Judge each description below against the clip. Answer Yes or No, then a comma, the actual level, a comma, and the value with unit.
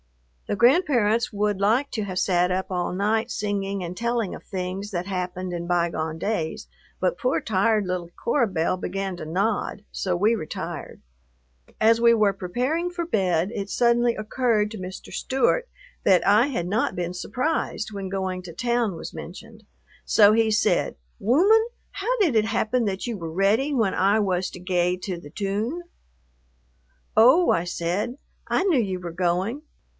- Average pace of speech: Yes, average, 170 wpm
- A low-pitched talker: No, high, 205 Hz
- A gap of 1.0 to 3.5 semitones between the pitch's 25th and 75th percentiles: No, average, 4.4 semitones